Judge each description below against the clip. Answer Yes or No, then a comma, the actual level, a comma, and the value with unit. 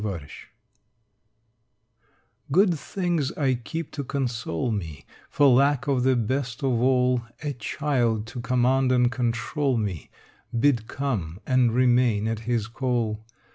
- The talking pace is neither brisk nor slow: No, slow, 130 wpm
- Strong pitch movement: No, average, 3.1 semitones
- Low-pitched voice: Yes, low, 125 Hz